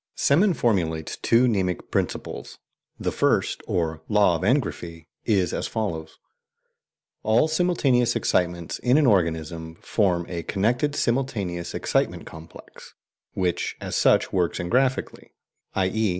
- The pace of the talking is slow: Yes, slow, 120 wpm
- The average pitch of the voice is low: Yes, very low, 95 Hz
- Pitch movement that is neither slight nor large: No, wide, 6.3 semitones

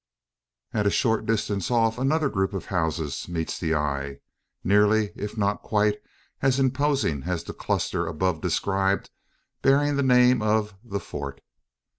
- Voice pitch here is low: Yes, low, 105 Hz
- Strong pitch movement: Yes, wide, 6.0 semitones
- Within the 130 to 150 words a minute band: Yes, average, 145 wpm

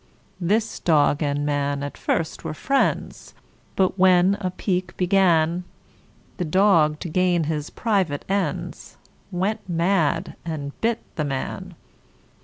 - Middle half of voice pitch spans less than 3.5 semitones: No, average, 4.1 semitones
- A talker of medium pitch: Yes, medium, 175 Hz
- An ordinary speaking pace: No, slow, 125 wpm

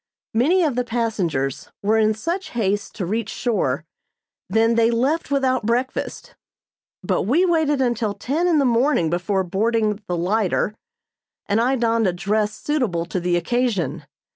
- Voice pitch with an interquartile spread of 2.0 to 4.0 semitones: No, average, 4.9 semitones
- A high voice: Yes, high, 225 Hz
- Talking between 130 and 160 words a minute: Yes, average, 155 wpm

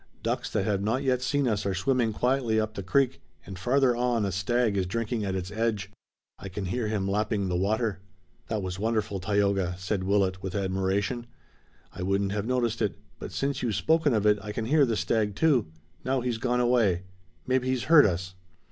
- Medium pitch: No, low, 105 Hz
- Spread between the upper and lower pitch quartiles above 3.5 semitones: Yes, average, 4.0 semitones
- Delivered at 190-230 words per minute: Yes, average, 200 wpm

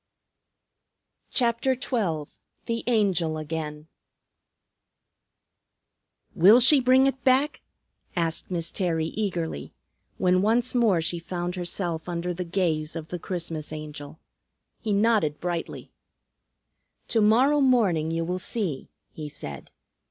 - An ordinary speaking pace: No, slow, 115 wpm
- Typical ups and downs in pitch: No, wide, 6.0 semitones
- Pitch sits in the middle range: Yes, medium, 180 Hz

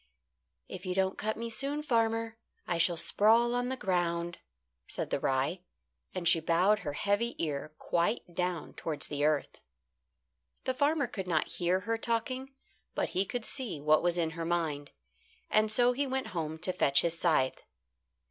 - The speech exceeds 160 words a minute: Yes, average, 170 wpm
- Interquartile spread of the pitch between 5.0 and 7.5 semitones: Yes, wide, 5.5 semitones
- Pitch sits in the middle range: Yes, medium, 180 Hz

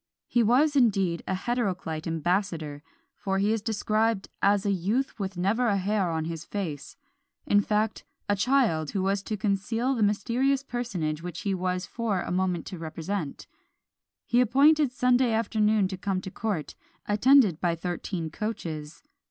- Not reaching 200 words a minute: Yes, average, 160 wpm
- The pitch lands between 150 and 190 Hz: No, high, 200 Hz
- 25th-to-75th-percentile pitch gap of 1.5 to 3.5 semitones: No, average, 4.3 semitones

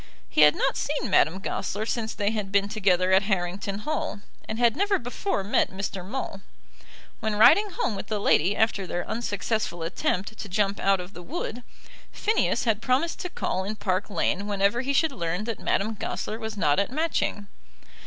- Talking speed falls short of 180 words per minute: No, average, 185 wpm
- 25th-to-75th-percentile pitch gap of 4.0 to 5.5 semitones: No, average, 3.4 semitones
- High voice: Yes, high, 205 Hz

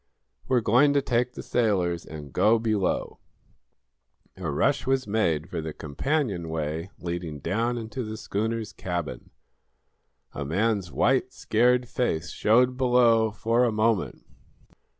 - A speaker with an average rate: No, slow, 130 wpm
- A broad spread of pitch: Yes, wide, 6.0 semitones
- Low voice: Yes, low, 110 Hz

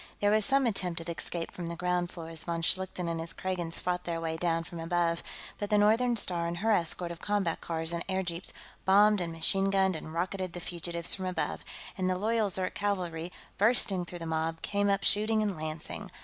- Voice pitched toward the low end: No, medium, 180 Hz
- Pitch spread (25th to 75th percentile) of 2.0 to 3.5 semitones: Yes, average, 2.9 semitones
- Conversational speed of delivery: No, fast, 215 wpm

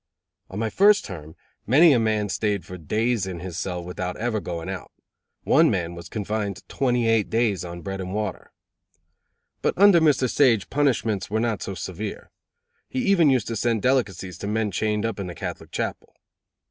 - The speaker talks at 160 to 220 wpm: Yes, average, 185 wpm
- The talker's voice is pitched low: Yes, low, 105 Hz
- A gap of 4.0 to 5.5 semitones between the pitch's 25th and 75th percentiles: Yes, average, 4.4 semitones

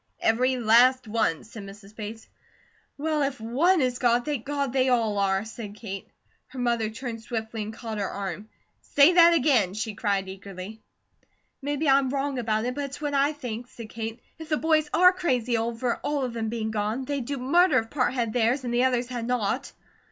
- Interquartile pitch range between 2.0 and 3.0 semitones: No, average, 3.8 semitones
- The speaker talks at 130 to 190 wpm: No, average, 200 wpm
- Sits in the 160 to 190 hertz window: No, high, 240 Hz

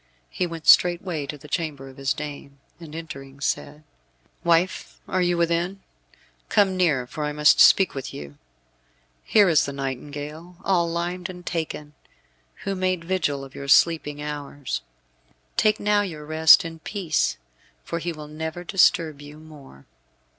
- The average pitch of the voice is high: No, medium, 160 Hz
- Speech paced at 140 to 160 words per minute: Yes, average, 155 wpm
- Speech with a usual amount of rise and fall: Yes, average, 3.3 semitones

